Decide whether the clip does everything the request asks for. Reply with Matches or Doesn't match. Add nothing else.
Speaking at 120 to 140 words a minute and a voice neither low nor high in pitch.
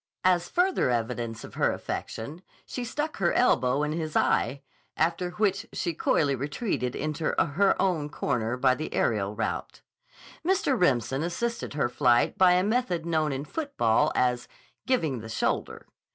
Doesn't match